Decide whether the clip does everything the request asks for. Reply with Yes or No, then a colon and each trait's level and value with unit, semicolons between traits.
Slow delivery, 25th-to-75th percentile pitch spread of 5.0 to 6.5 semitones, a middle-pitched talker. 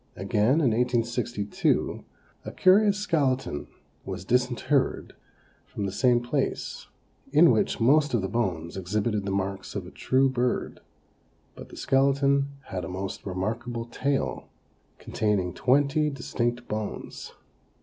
No: slow, 125 wpm; wide, 5.4 semitones; low, 120 Hz